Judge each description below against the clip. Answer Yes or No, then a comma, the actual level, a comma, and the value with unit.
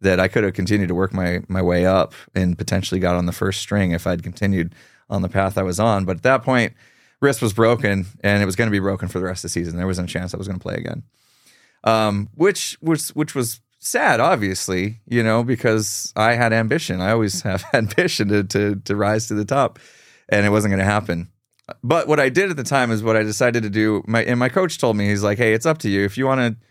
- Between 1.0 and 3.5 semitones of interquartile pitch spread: No, average, 3.9 semitones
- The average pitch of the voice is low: Yes, low, 105 Hz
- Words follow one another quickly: Yes, fast, 265 wpm